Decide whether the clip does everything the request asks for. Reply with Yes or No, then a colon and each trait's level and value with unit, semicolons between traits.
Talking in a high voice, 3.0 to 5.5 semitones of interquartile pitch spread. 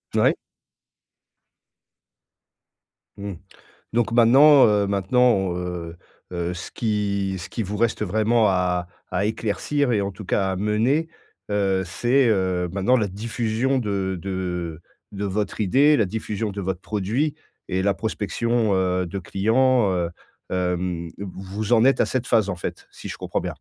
No: low, 100 Hz; average, 3.6 semitones